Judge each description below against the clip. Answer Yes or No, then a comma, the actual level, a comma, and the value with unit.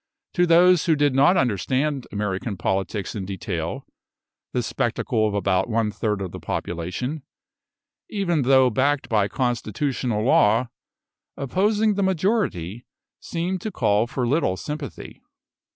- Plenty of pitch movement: Yes, wide, 7.5 semitones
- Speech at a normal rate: No, slow, 130 wpm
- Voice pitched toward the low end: Yes, low, 125 Hz